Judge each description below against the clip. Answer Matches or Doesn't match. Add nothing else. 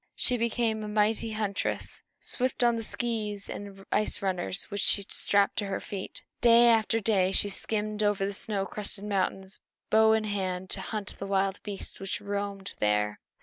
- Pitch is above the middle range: Matches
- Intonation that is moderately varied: Doesn't match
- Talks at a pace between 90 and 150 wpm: Doesn't match